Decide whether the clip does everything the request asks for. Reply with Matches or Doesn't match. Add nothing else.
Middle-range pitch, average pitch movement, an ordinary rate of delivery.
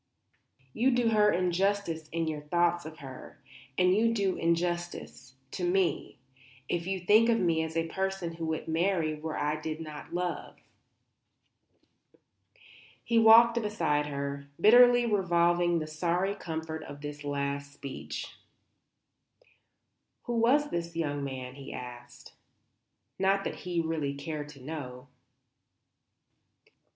Doesn't match